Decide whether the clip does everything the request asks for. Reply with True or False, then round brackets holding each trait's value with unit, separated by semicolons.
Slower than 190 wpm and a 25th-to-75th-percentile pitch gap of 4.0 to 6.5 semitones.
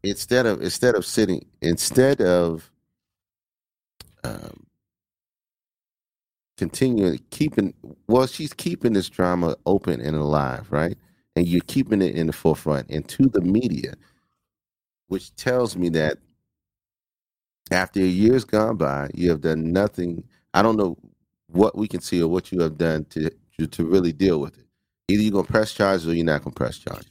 True (160 wpm; 4.4 semitones)